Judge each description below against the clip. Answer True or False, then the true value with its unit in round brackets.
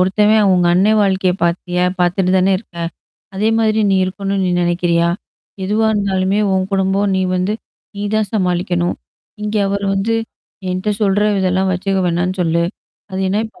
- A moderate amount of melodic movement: False (2.0 semitones)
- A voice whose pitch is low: False (190 Hz)